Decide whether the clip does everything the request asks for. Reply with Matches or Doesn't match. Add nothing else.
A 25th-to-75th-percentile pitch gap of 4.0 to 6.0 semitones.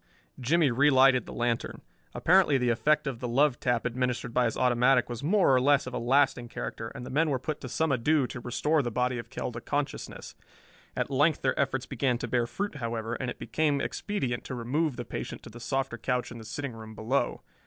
Doesn't match